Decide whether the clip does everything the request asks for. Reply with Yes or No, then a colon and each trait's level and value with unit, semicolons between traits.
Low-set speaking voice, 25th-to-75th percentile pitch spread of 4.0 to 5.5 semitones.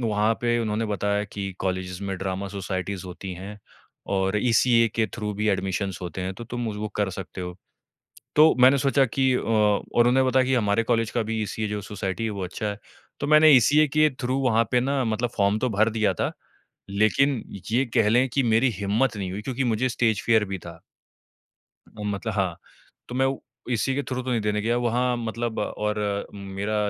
No: low, 110 Hz; average, 3.5 semitones